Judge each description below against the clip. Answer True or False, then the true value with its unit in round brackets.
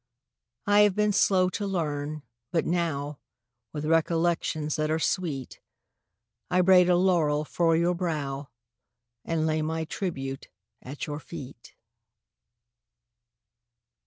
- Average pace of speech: False (120 wpm)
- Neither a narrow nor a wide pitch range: True (3.2 semitones)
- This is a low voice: False (160 Hz)